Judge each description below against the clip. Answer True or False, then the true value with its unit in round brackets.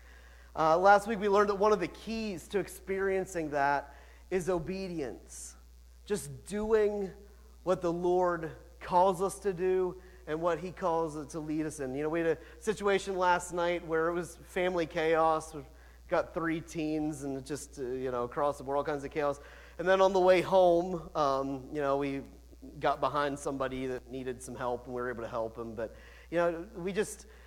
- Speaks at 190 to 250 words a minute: True (200 wpm)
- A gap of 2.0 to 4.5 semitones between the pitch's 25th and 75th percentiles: False (5.1 semitones)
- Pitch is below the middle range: False (160 Hz)